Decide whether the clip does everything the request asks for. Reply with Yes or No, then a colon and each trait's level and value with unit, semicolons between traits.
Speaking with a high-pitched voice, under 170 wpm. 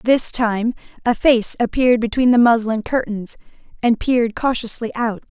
Yes: high, 230 Hz; average, 145 wpm